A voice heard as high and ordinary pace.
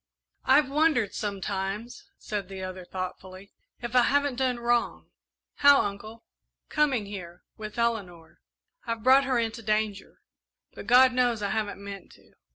Yes: high, 220 Hz; average, 145 wpm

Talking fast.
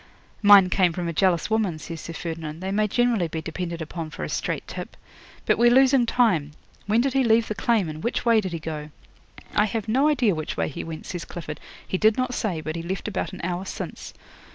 Yes: fast, 230 wpm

